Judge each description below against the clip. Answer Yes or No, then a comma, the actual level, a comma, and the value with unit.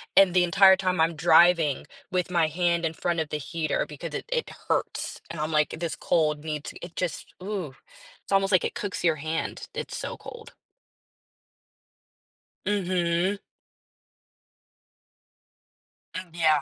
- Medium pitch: Yes, medium, 170 Hz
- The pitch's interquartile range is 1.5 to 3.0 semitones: Yes, average, 2.7 semitones